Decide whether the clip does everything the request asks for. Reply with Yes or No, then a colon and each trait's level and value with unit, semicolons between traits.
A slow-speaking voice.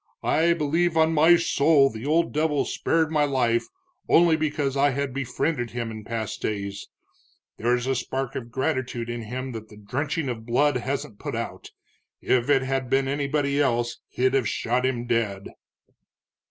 No: average, 165 wpm